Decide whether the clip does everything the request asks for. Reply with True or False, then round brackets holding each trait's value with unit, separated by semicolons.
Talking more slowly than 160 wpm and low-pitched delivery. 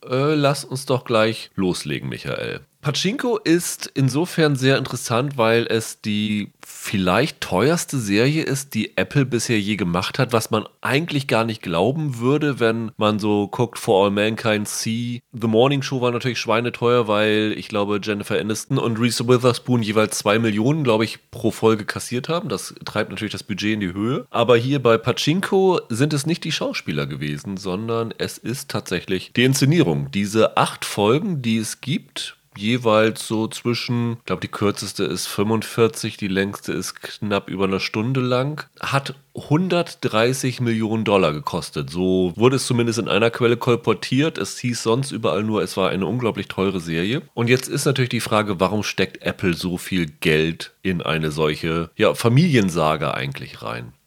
False (170 wpm; 115 Hz)